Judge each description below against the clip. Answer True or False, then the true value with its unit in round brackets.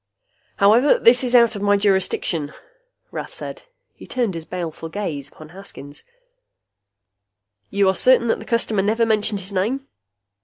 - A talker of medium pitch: False (200 Hz)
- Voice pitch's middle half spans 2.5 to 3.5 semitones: False (4.2 semitones)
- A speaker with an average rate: True (155 wpm)